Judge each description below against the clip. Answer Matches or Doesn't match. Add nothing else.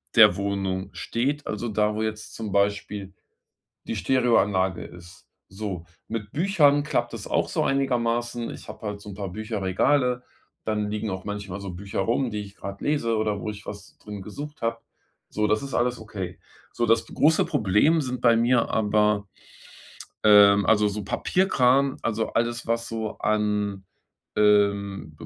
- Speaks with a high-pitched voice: Doesn't match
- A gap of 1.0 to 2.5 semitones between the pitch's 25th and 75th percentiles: Doesn't match